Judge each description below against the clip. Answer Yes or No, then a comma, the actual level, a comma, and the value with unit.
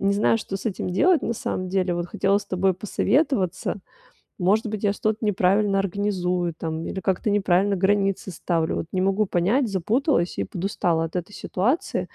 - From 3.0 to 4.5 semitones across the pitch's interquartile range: No, narrow, 2.5 semitones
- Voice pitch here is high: Yes, high, 195 Hz